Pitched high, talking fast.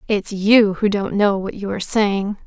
Yes: high, 200 Hz; fast, 220 wpm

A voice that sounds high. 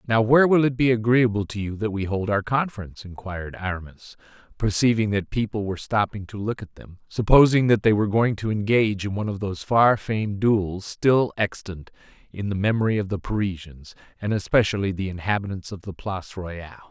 No: low, 105 Hz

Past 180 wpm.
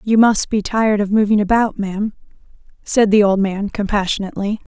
No: average, 165 wpm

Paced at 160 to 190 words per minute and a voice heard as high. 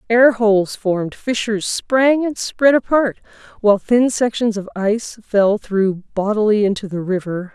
No: average, 150 wpm; high, 215 Hz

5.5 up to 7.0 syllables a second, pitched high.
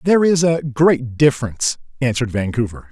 No: 5.9 syllables/s; low, 135 Hz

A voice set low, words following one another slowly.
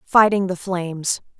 No: medium, 185 Hz; slow, 130 wpm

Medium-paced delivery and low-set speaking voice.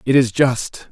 Yes: average, 195 wpm; low, 125 Hz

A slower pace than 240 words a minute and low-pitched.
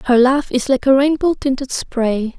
No: average, 200 wpm; very high, 260 Hz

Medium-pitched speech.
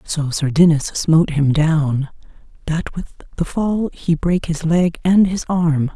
Yes: medium, 160 Hz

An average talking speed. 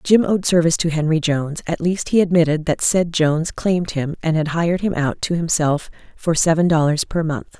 No: fast, 215 wpm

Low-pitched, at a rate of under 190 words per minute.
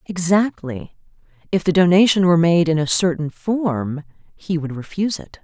No: medium, 170 Hz; average, 155 wpm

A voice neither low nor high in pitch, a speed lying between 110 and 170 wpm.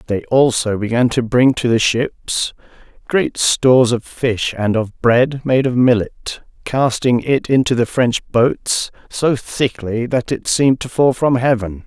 No: low, 125 Hz; average, 165 wpm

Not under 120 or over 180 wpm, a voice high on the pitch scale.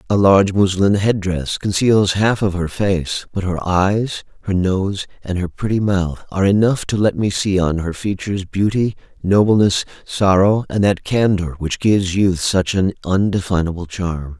No: average, 170 wpm; very low, 95 Hz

